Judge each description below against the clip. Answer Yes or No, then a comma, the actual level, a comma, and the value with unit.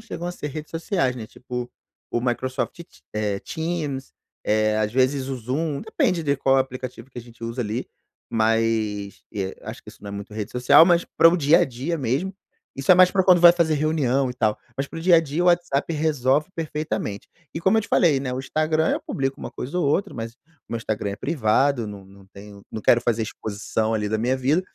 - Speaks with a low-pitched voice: Yes, low, 130 Hz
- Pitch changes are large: Yes, wide, 5.9 semitones